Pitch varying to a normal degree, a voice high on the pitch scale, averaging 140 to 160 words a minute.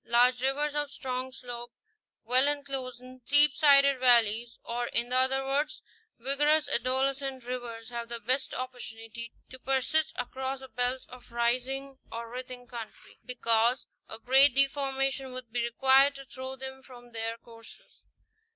No: narrow, 2.1 semitones; very high, 255 Hz; average, 150 wpm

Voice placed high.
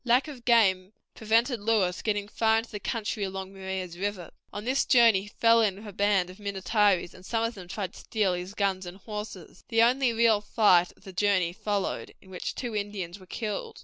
Yes: high, 205 Hz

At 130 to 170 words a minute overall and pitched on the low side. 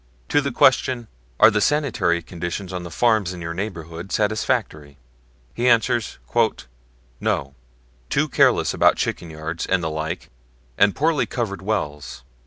Yes: average, 140 wpm; very low, 95 Hz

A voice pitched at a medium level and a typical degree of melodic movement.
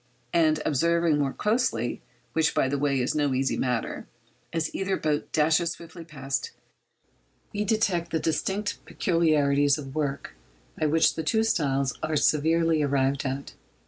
Yes: medium, 155 Hz; average, 3.3 semitones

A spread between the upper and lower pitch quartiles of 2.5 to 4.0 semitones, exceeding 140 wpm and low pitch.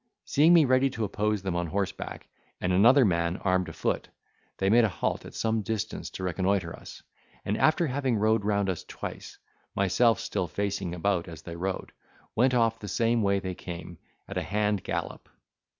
Yes: average, 3.7 semitones; average, 185 wpm; low, 100 Hz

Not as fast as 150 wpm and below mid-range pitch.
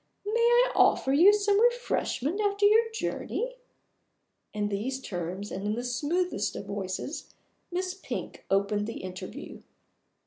No: slow, 135 wpm; very high, 290 Hz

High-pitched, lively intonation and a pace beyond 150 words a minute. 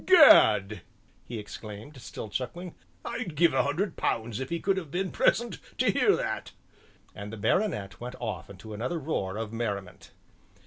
No: low, 120 Hz; wide, 8.4 semitones; average, 165 wpm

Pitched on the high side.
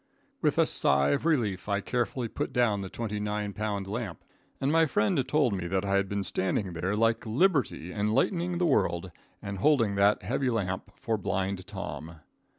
No: low, 105 Hz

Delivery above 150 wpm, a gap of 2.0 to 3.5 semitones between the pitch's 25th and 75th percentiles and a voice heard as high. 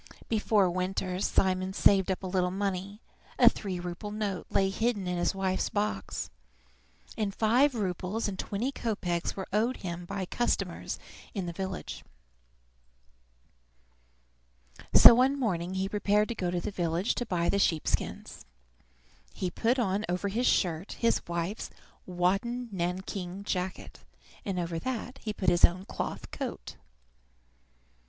No: average, 145 wpm; average, 2.8 semitones; high, 195 Hz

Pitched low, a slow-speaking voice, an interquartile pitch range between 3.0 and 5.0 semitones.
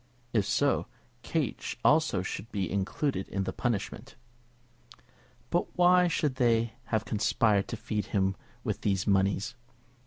Yes: low, 110 Hz; slow, 130 wpm; average, 3.8 semitones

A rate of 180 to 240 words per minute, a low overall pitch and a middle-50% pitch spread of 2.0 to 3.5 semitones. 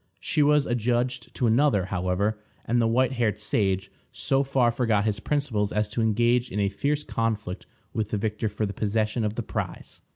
Yes: average, 190 wpm; low, 110 Hz; average, 2.9 semitones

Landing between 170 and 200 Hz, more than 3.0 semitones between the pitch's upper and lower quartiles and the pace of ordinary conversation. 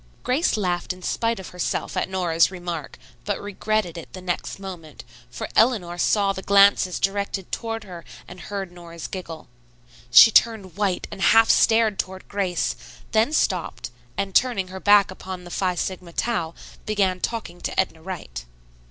No: high, 190 Hz; average, 2.7 semitones; average, 160 wpm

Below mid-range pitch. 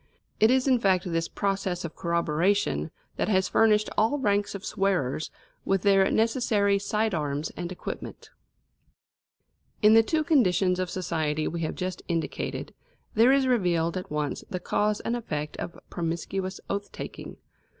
No: high, 190 Hz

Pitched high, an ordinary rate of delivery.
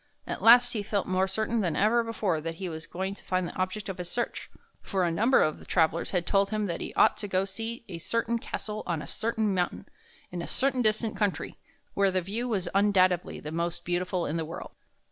No: high, 195 Hz; fast, 230 wpm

